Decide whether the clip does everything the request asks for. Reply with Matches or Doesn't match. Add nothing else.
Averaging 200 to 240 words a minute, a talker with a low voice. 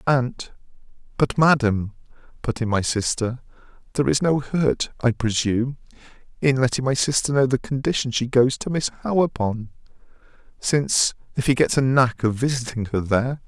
Doesn't match